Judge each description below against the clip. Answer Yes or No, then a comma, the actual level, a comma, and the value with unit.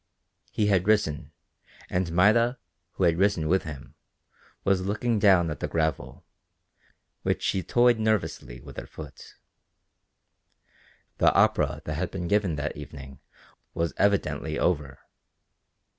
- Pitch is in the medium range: No, very low, 90 Hz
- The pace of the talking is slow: Yes, slow, 130 wpm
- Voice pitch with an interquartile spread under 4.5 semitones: No, average, 4.9 semitones